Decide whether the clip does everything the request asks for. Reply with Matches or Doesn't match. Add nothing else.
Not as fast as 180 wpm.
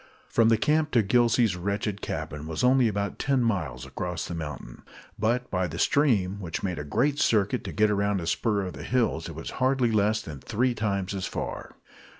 Doesn't match